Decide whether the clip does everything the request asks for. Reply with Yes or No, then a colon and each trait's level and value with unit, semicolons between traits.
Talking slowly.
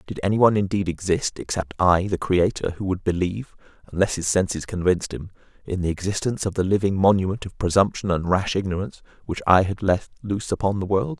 No: average, 200 wpm